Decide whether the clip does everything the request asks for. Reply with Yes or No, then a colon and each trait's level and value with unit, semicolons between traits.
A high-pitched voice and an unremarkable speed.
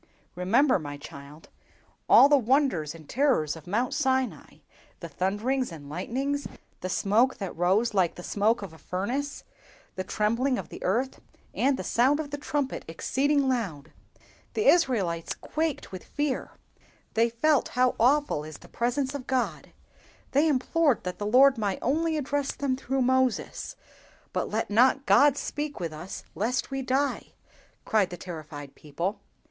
Yes: high, 245 Hz; average, 155 wpm